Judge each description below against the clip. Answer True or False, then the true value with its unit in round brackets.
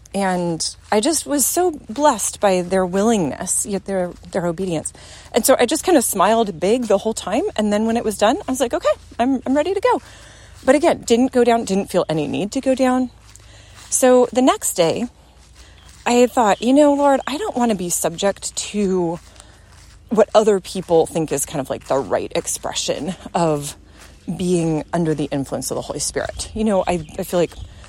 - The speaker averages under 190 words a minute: False (200 wpm)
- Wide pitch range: True (6.6 semitones)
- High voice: True (205 Hz)